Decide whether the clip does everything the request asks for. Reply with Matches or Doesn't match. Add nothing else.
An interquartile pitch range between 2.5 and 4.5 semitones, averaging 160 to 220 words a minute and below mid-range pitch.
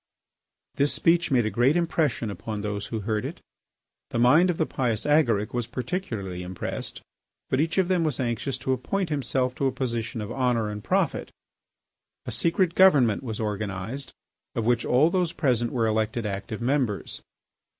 Doesn't match